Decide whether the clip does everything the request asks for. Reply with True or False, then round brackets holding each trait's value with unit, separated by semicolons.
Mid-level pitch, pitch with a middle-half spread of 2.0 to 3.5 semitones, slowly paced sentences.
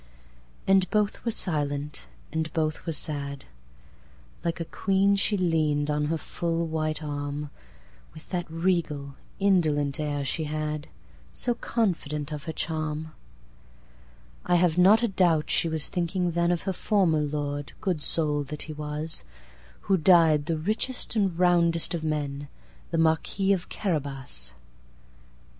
True (155 Hz; 3.2 semitones; 125 wpm)